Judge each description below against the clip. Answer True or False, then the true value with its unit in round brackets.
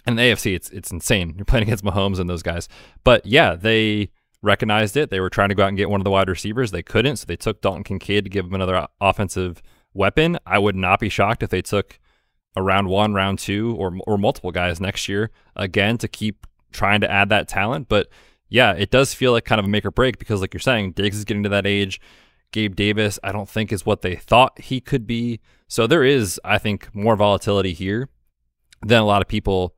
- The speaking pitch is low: True (100 Hz)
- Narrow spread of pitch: True (2.3 semitones)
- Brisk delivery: True (240 wpm)